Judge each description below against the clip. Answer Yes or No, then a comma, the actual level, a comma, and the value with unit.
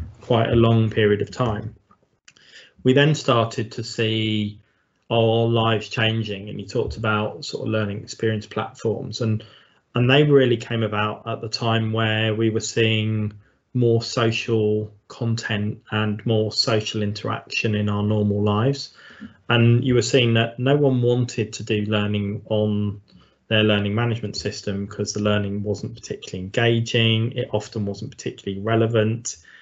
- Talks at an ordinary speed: Yes, average, 150 wpm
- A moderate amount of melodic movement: No, narrow, 1.7 semitones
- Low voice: Yes, low, 110 Hz